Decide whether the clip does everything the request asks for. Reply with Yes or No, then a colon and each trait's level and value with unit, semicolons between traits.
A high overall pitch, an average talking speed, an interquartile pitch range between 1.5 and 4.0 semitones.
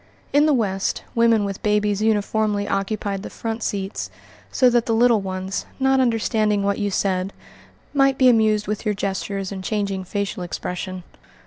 Yes: high, 210 Hz; average, 160 wpm; narrow, 2.4 semitones